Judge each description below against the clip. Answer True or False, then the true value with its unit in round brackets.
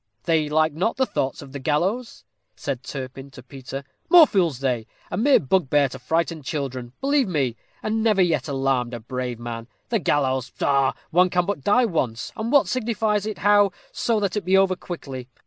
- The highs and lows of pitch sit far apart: True (7.5 semitones)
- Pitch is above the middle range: False (155 Hz)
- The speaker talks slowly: False (190 wpm)